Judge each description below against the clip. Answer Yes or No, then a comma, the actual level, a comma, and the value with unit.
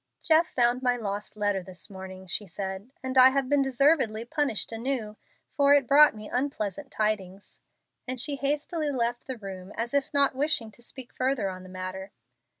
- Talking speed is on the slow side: No, average, 180 wpm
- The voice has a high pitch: Yes, high, 240 Hz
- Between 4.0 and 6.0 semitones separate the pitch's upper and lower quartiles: Yes, wide, 5.5 semitones